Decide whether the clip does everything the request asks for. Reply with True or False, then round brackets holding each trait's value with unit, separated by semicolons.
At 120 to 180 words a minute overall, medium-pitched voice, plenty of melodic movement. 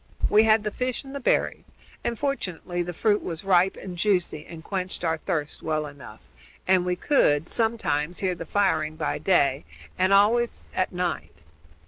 False (170 wpm; 180 Hz; 4.7 semitones)